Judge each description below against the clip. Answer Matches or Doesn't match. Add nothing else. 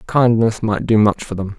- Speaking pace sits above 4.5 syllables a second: Matches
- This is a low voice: Matches